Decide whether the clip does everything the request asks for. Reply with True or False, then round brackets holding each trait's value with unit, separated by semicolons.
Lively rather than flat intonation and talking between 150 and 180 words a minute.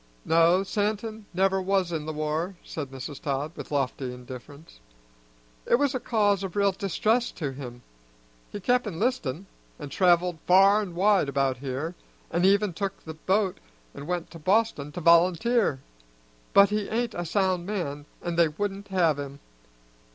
False (5.0 semitones; 160 wpm)